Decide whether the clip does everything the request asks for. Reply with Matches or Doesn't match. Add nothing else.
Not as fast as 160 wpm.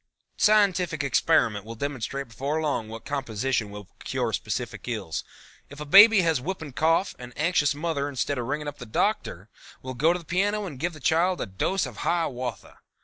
Doesn't match